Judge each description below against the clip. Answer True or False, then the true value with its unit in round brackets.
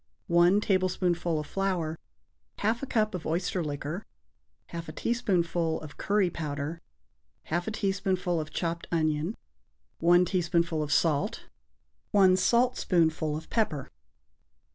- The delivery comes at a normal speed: False (120 wpm)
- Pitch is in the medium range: True (175 Hz)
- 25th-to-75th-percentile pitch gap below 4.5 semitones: True (3.3 semitones)